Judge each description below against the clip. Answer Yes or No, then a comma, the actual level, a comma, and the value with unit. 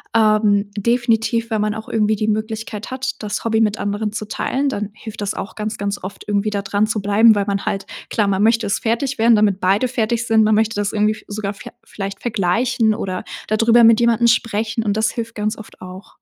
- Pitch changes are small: Yes, narrow, 1.8 semitones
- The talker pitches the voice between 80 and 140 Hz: No, high, 215 Hz